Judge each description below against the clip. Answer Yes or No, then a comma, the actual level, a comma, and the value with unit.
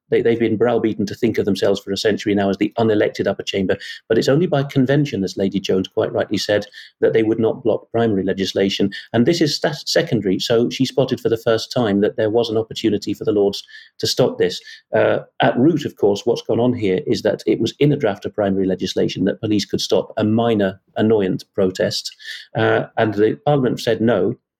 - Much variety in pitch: No, average, 4.6 semitones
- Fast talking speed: Yes, fast, 220 wpm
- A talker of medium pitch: No, low, 110 Hz